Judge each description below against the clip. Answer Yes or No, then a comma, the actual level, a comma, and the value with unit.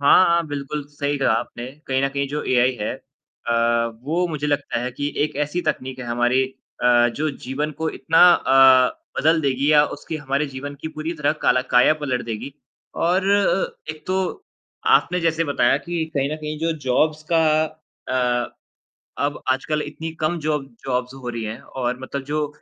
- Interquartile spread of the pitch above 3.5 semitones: No, average, 3.2 semitones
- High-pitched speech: No, medium, 145 Hz